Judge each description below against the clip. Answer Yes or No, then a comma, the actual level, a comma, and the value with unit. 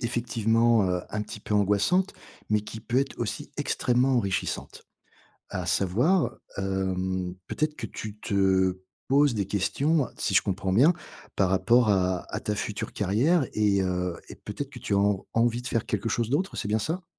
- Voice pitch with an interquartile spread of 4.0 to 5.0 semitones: Yes, average, 4.3 semitones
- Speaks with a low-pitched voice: Yes, low, 105 Hz